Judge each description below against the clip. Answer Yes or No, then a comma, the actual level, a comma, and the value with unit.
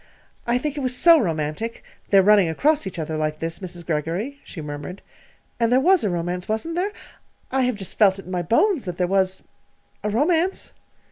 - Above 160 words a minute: Yes, average, 195 wpm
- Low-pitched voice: No, high, 195 Hz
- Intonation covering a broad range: Yes, wide, 7.3 semitones